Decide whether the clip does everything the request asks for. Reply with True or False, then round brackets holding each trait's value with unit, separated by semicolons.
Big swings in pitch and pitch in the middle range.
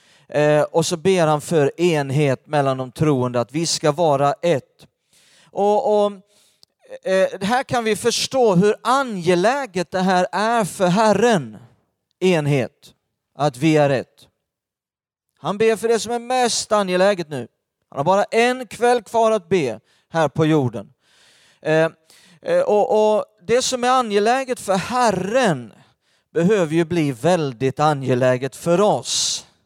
True (6.9 semitones; 180 Hz)